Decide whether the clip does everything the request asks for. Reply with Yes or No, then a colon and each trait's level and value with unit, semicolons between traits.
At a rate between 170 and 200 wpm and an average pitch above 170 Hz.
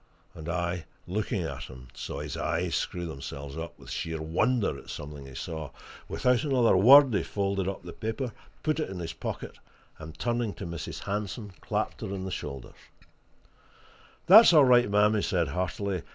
No: average, 180 wpm; very low, 95 Hz